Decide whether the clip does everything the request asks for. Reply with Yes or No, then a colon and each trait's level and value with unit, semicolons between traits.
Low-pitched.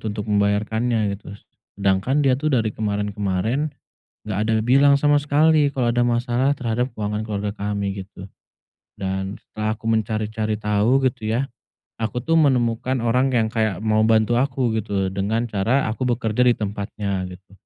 Yes: low, 110 Hz